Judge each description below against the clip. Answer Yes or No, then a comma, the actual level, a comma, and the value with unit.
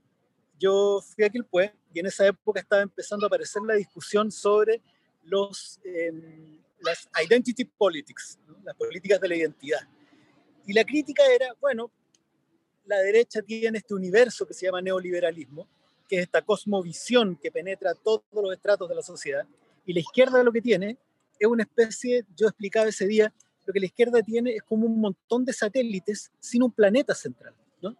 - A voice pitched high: Yes, high, 210 Hz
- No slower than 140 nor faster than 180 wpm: Yes, average, 175 wpm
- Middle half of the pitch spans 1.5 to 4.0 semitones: Yes, average, 3.7 semitones